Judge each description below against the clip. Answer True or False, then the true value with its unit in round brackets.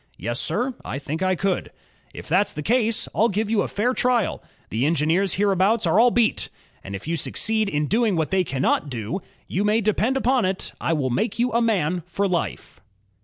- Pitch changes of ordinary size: False (6.0 semitones)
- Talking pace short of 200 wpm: False (205 wpm)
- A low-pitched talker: False (195 Hz)